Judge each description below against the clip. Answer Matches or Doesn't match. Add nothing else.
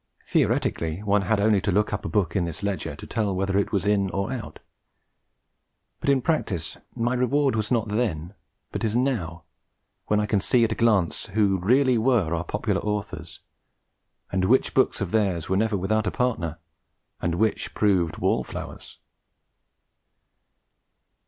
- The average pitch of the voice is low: Matches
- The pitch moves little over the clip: Doesn't match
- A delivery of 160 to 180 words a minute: Matches